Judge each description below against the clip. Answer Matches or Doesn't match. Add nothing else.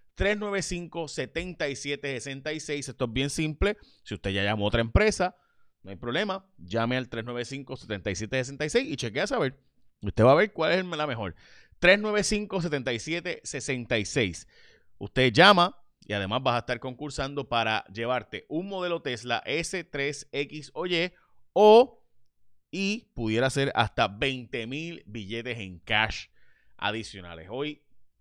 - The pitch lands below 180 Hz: Matches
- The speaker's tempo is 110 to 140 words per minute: Matches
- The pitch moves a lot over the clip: Matches